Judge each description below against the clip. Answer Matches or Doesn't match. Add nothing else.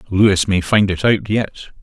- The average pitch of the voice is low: Matches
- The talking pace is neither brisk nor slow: Matches